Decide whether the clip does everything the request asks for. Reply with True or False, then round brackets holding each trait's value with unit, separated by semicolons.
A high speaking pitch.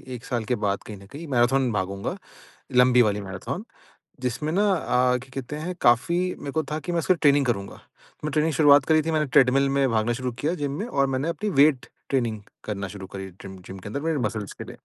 False (130 Hz)